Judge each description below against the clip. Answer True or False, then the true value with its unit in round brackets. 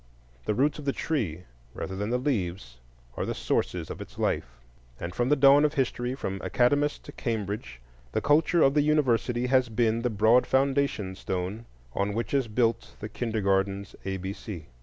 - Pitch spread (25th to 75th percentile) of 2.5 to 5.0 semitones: False (5.6 semitones)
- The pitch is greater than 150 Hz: False (115 Hz)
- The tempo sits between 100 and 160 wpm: False (180 wpm)